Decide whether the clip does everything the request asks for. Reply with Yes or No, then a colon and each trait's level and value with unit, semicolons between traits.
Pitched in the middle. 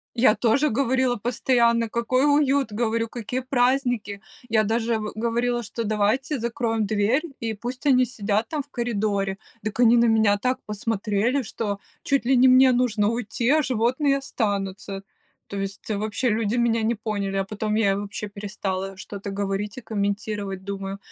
No: high, 225 Hz